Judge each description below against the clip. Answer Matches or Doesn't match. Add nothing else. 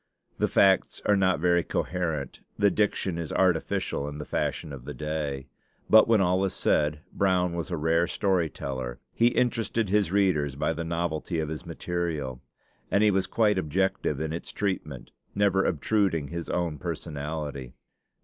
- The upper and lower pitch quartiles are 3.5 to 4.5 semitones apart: Matches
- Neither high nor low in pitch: Doesn't match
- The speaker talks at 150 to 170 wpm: Matches